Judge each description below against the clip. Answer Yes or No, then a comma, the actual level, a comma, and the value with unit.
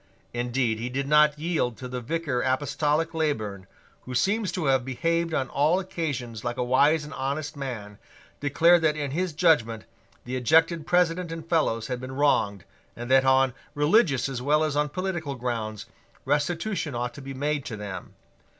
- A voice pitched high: No, medium, 145 Hz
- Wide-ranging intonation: No, average, 4.5 semitones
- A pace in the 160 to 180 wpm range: Yes, average, 175 wpm